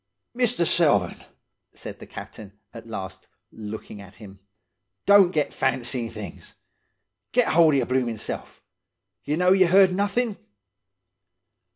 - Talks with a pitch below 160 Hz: Yes, low, 135 Hz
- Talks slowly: Yes, slow, 130 wpm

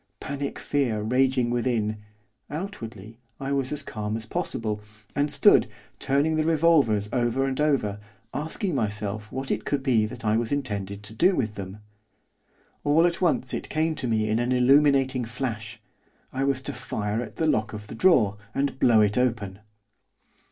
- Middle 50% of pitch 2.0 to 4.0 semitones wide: No, average, 4.8 semitones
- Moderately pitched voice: No, low, 125 Hz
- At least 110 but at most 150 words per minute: No, average, 165 wpm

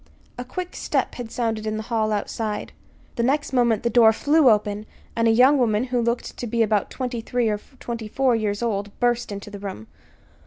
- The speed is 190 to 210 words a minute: Yes, fast, 205 wpm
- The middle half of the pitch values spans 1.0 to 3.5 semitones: Yes, narrow, 2.5 semitones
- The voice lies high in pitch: Yes, high, 230 Hz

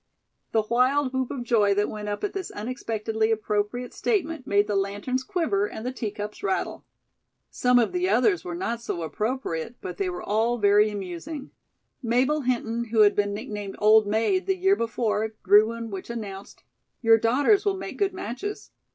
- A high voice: Yes, high, 225 Hz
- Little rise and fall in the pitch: No, average, 3.9 semitones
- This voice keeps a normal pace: Yes, average, 175 wpm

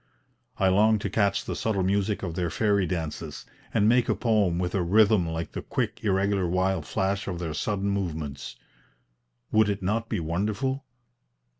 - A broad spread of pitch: No, average, 3.3 semitones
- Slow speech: No, average, 170 wpm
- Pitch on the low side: Yes, very low, 95 Hz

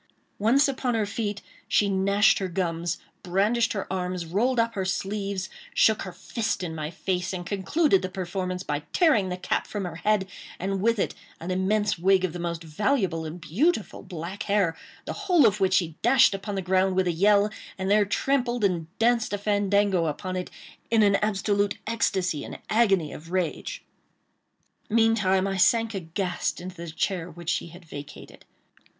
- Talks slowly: No, average, 180 wpm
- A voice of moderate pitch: No, high, 195 Hz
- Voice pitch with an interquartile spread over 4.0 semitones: No, average, 3.0 semitones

